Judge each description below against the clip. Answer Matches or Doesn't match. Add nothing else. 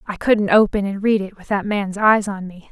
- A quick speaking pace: Matches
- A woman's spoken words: Matches